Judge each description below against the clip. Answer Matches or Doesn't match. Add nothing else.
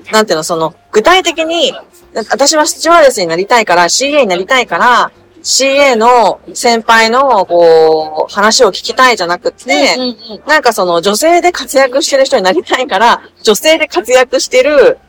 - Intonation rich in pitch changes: Matches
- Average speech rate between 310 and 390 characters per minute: Matches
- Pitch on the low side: Doesn't match